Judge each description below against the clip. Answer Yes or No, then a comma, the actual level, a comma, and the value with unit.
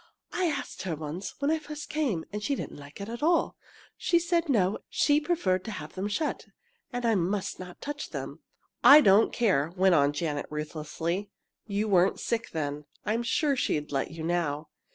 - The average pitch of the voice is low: No, high, 200 Hz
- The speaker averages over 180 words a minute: Yes, average, 190 wpm